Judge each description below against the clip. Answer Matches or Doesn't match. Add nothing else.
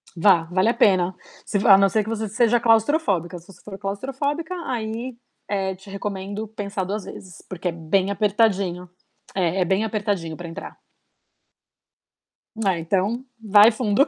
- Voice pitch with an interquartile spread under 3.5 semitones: Matches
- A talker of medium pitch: Doesn't match